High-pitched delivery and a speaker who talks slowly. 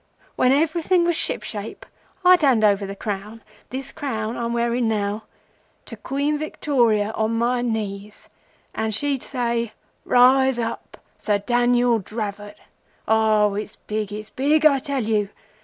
Yes: high, 230 Hz; slow, 130 wpm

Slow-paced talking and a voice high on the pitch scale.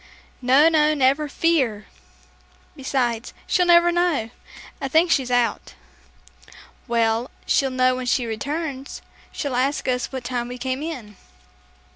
Yes: slow, 130 wpm; very high, 260 Hz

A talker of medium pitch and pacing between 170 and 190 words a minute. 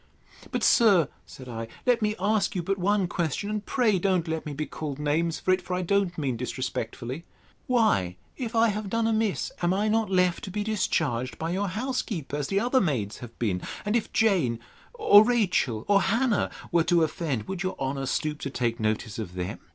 No: medium, 180 Hz; fast, 205 wpm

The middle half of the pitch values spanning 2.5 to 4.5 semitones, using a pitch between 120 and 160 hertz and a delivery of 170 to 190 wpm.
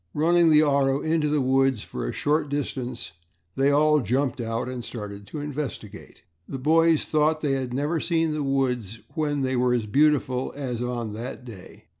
Yes: average, 3.6 semitones; low, 135 Hz; average, 180 wpm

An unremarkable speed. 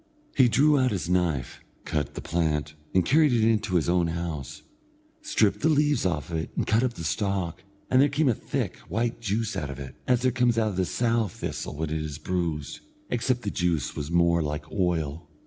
No: fast, 215 wpm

